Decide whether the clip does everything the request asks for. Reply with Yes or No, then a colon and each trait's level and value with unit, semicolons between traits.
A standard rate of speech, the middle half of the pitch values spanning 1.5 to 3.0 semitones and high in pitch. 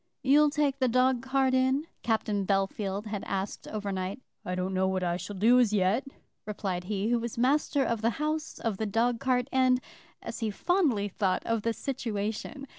No: average, 190 wpm; average, 4.6 semitones; high, 225 Hz